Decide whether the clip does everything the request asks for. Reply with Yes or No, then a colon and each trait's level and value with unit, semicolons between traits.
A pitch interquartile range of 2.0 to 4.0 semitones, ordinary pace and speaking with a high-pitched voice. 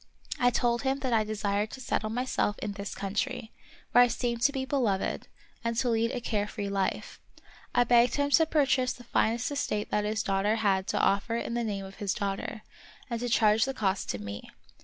No: average, 3.3 semitones; fast, 215 wpm; high, 225 Hz